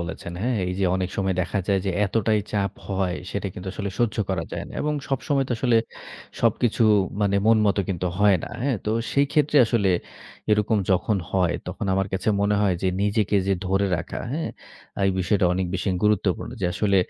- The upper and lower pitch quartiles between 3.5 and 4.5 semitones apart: No, average, 2.8 semitones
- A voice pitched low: Yes, low, 100 Hz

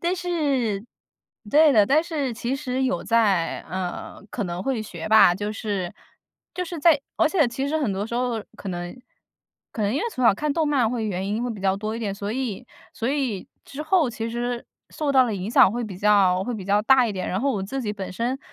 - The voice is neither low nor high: No, high, 230 Hz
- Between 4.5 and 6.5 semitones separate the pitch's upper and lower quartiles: Yes, average, 5.1 semitones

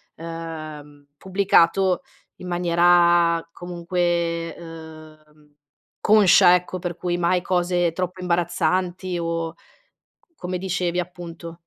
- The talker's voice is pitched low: No, medium, 175 Hz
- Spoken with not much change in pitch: Yes, narrow, 1.4 semitones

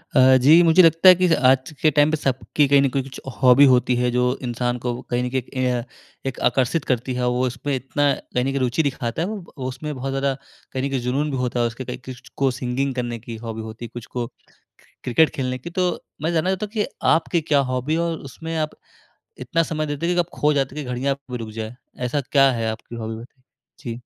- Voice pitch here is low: Yes, low, 130 Hz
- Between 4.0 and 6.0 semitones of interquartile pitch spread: No, average, 3.5 semitones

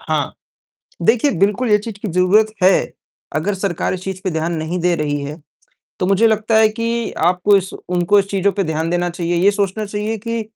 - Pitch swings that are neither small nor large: Yes, average, 3.6 semitones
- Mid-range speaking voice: No, high, 195 Hz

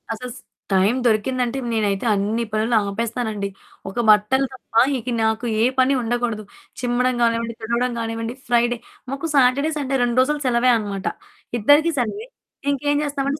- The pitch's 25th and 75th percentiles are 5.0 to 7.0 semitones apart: No, average, 2.8 semitones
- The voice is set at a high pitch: Yes, high, 240 Hz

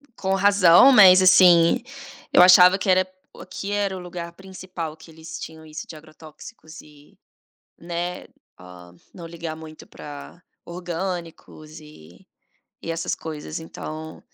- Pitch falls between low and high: Yes, medium, 170 Hz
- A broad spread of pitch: No, narrow, 2.6 semitones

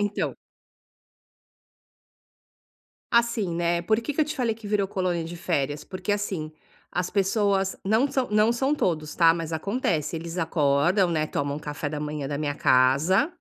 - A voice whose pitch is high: No, medium, 175 Hz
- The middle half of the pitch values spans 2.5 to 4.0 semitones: No, average, 5.3 semitones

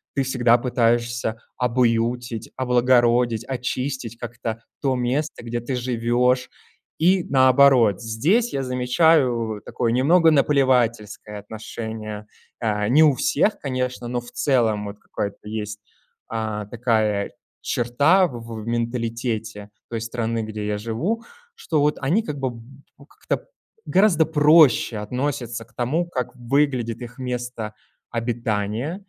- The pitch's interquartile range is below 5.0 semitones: Yes, average, 2.8 semitones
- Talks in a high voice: No, low, 120 Hz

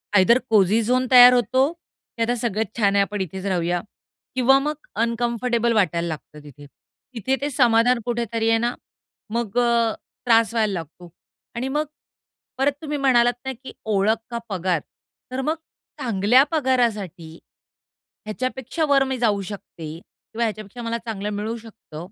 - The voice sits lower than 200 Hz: No, high, 230 Hz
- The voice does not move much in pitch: No, average, 3.7 semitones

